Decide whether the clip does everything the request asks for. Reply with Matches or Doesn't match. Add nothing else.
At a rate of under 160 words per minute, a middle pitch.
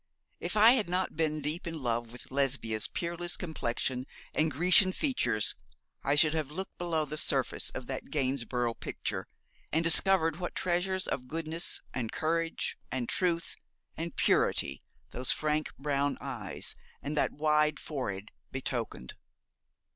Matches